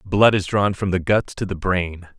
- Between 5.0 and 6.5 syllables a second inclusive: No, 4.4 syllables/s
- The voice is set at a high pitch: No, very low, 95 Hz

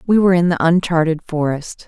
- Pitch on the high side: No, medium, 170 Hz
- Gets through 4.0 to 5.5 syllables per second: No, 5.9 syllables/s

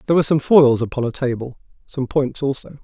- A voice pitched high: No, low, 135 Hz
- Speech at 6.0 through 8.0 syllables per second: Yes, 6.3 syllables/s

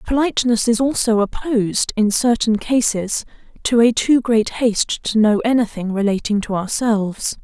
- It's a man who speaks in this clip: No, female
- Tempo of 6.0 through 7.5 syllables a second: No, 4.8 syllables/s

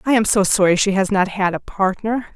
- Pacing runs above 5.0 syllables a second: Yes, 5.4 syllables/s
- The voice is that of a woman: Yes, female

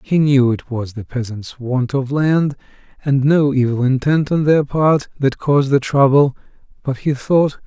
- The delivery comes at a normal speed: Yes, average, 180 wpm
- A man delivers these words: Yes, male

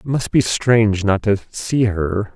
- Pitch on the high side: No, low, 105 Hz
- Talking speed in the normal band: Yes, average, 180 wpm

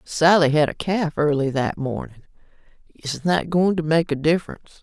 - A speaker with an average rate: Yes, average, 175 wpm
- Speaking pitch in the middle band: Yes, medium, 160 Hz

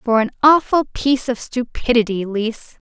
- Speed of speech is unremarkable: Yes, average, 145 wpm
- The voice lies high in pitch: Yes, high, 240 Hz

